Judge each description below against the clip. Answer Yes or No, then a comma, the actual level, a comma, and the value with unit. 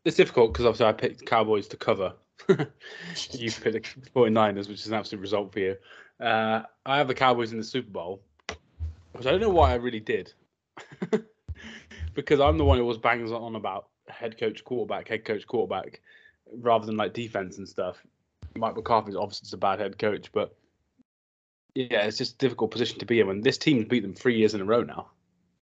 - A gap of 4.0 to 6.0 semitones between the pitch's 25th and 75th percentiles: Yes, average, 4.9 semitones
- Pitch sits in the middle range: No, low, 110 Hz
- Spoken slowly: No, fast, 205 wpm